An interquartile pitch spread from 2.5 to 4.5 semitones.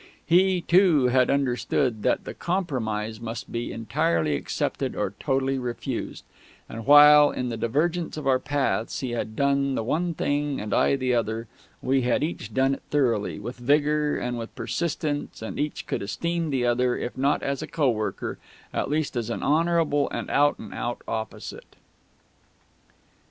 Yes: average, 4.0 semitones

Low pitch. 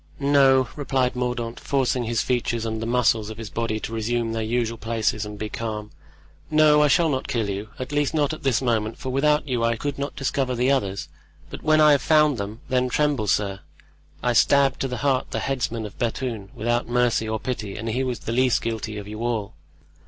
Yes: low, 120 Hz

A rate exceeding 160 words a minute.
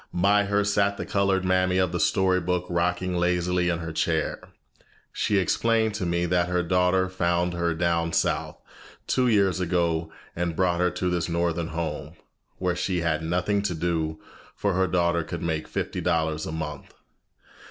Yes: average, 175 wpm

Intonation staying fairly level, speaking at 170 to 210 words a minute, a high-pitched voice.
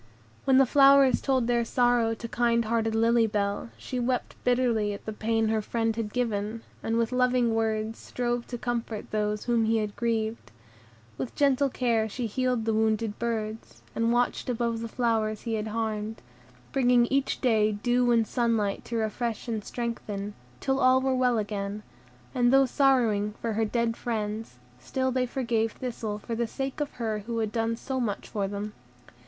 Yes: narrow, 2.1 semitones; average, 180 wpm; high, 230 Hz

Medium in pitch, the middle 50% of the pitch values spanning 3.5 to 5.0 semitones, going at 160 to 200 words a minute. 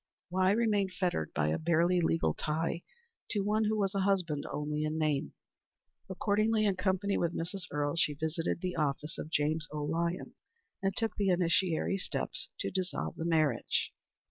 Yes: medium, 170 Hz; average, 3.9 semitones; average, 170 wpm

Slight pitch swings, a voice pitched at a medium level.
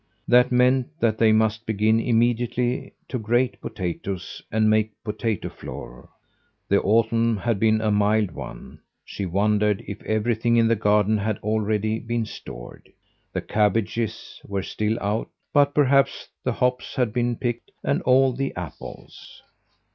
No: narrow, 2.3 semitones; low, 110 Hz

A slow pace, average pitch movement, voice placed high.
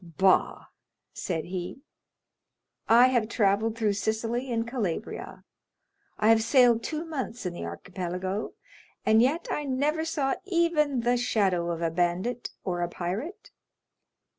No: slow, 130 wpm; wide, 6.2 semitones; high, 225 Hz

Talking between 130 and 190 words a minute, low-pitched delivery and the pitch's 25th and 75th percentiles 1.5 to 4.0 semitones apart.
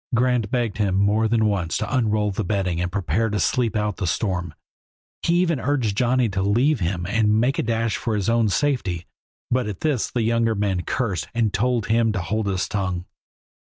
No: average, 200 wpm; low, 110 Hz; average, 3.3 semitones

